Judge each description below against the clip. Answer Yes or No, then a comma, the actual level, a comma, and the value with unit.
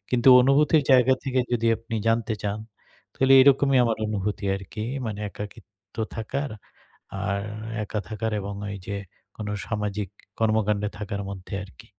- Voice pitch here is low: Yes, low, 110 Hz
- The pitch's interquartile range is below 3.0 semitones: No, average, 3.6 semitones